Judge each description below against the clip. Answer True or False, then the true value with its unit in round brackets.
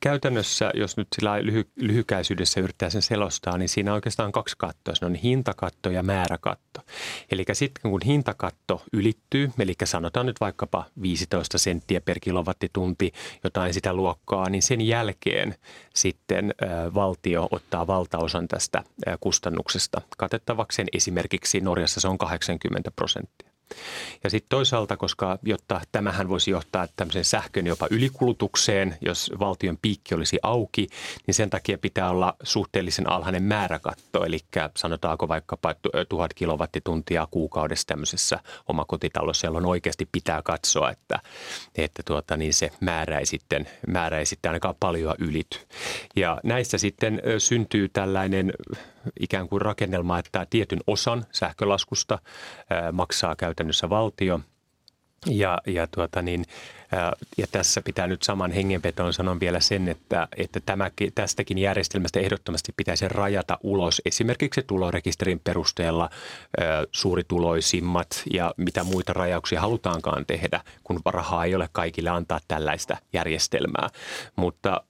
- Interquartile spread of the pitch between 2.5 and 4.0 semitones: True (2.9 semitones)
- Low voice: True (95 Hz)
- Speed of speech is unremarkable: True (130 wpm)